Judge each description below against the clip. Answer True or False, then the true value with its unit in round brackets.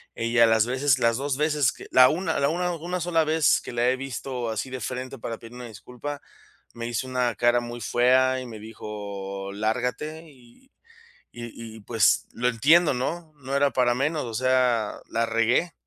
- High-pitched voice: False (125 Hz)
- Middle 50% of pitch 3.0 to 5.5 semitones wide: True (3.5 semitones)